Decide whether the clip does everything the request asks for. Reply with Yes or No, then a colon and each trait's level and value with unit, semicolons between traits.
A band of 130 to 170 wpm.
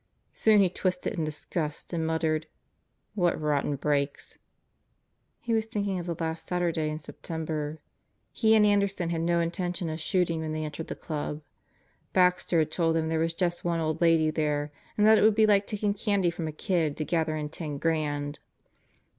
No: average, 185 wpm